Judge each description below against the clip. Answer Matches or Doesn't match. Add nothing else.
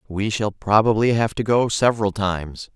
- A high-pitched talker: Doesn't match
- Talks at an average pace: Matches